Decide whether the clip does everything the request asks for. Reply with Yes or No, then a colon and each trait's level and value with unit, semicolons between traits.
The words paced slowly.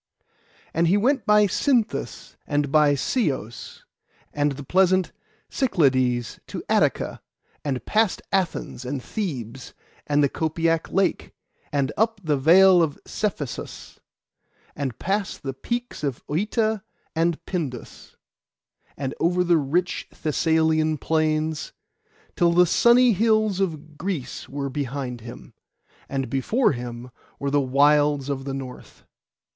Yes: slow, 125 wpm